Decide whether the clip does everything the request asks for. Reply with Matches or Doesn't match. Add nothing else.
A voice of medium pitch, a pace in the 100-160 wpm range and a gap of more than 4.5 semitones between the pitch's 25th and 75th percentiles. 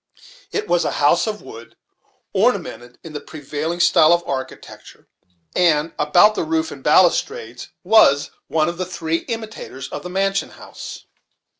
Matches